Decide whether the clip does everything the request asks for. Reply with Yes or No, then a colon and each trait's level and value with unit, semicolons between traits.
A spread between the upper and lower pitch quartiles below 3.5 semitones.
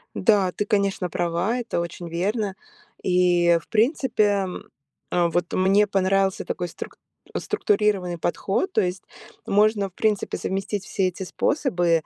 Yes: average, 2.8 semitones